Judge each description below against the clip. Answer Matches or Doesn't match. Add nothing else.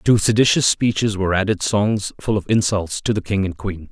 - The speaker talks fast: Matches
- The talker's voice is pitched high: Doesn't match